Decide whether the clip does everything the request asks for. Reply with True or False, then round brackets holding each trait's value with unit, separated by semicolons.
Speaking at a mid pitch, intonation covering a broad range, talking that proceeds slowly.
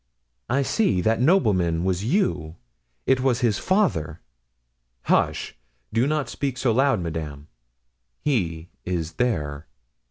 False (110 Hz; 8.4 semitones; 120 wpm)